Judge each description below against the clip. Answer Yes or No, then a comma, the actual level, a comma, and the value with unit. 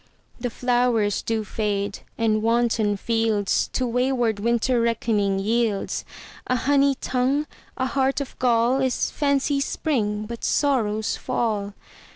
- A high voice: Yes, high, 235 Hz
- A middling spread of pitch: Yes, average, 3.3 semitones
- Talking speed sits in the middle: No, slow, 110 wpm